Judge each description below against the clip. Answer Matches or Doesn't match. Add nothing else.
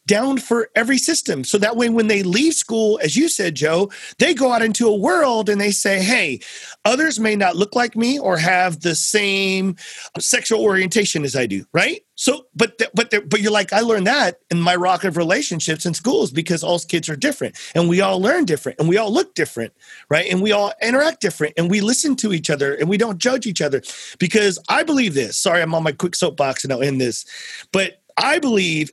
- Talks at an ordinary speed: Doesn't match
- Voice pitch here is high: Matches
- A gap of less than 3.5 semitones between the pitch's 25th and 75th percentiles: Doesn't match